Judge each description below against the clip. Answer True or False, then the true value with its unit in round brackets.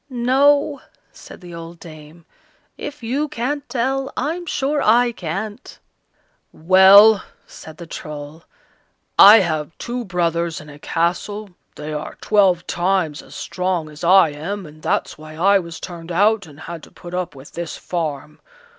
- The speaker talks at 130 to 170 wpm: True (155 wpm)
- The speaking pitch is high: False (180 Hz)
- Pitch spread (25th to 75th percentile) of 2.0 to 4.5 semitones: False (5.6 semitones)